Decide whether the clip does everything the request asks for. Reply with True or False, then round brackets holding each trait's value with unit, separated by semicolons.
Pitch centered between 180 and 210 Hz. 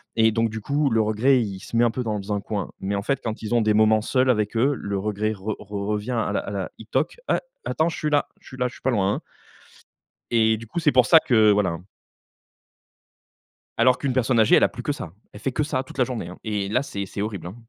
False (110 Hz)